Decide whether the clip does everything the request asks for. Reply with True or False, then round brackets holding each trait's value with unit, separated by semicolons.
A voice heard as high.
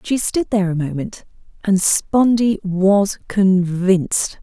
True (195 Hz)